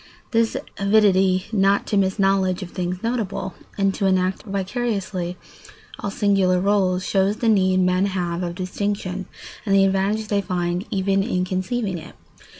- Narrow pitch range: Yes, narrow, 1.6 semitones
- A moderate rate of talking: Yes, average, 150 wpm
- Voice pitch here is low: No, high, 195 Hz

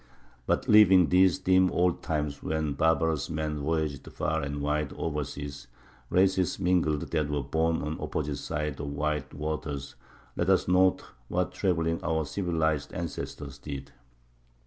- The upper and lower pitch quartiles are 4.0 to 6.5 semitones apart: No, average, 3.1 semitones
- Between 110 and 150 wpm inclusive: Yes, average, 145 wpm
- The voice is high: No, very low, 80 Hz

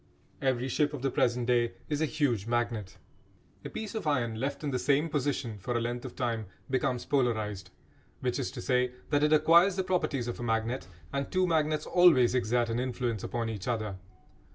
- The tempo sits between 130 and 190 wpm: No, average, 200 wpm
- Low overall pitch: Yes, low, 125 Hz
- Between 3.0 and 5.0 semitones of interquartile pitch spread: Yes, average, 3.8 semitones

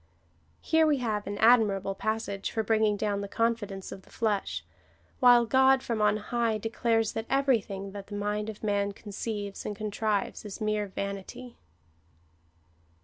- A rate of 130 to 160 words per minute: Yes, average, 150 wpm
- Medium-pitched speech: No, high, 215 Hz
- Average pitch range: No, narrow, 2.3 semitones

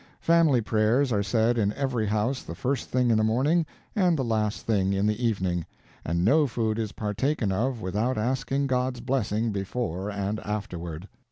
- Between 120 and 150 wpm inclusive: No, average, 175 wpm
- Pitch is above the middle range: No, low, 110 Hz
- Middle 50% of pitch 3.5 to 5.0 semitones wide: Yes, average, 3.9 semitones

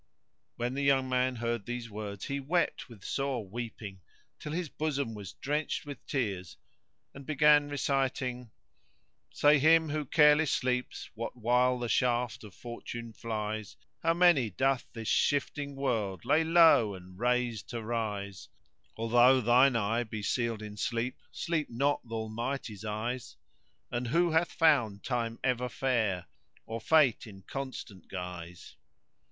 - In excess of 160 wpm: No, average, 145 wpm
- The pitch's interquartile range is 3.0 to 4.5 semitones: Yes, average, 4.1 semitones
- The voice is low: Yes, low, 120 Hz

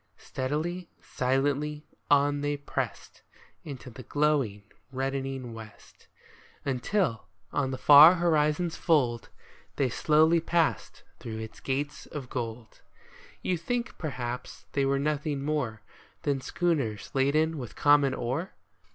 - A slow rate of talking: Yes, slow, 115 wpm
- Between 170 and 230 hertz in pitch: No, medium, 140 Hz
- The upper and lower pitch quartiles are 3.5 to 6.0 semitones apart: No, average, 3.1 semitones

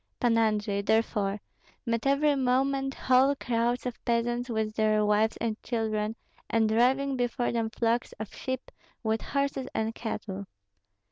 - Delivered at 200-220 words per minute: No, average, 140 wpm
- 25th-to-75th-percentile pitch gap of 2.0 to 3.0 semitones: Yes, average, 2.7 semitones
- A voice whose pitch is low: No, high, 230 Hz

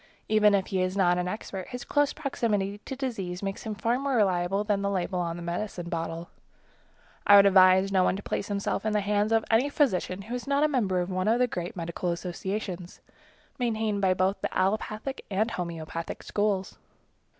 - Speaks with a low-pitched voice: No, high, 200 Hz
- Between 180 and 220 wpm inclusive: Yes, average, 200 wpm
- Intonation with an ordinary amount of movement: Yes, average, 3.0 semitones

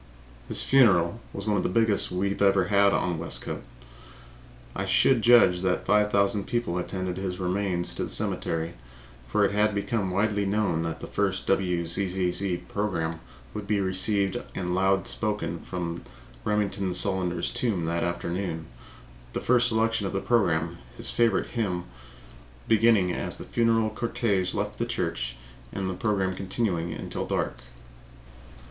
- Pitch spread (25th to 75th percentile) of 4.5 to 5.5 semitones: No, average, 2.9 semitones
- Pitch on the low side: Yes, very low, 95 Hz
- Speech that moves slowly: No, average, 150 wpm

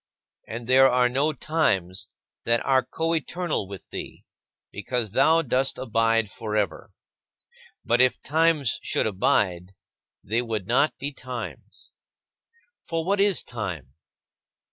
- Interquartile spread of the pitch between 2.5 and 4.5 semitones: No, wide, 5.4 semitones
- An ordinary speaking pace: No, slow, 120 wpm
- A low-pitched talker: Yes, low, 125 Hz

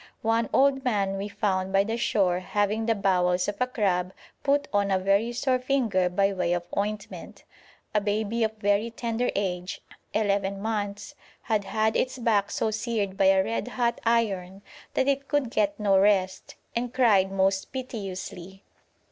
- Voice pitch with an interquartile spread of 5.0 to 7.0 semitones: No, average, 3.1 semitones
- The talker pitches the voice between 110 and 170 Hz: No, high, 205 Hz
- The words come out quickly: No, average, 165 wpm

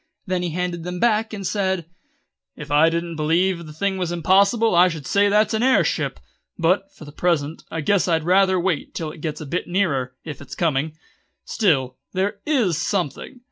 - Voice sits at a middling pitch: Yes, medium, 175 Hz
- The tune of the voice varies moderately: Yes, average, 3.8 semitones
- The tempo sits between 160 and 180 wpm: No, average, 195 wpm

